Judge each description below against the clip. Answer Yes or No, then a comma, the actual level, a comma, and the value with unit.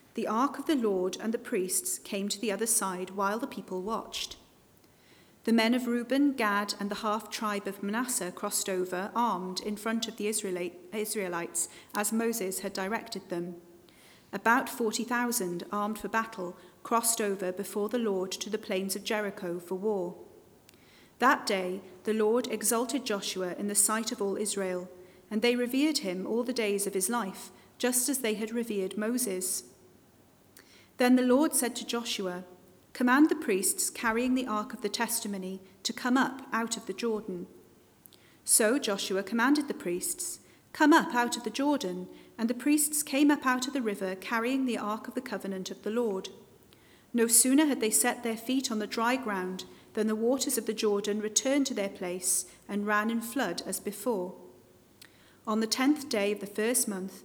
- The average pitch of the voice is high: Yes, high, 215 Hz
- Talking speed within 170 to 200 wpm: Yes, average, 180 wpm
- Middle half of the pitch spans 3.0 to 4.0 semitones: Yes, average, 3.7 semitones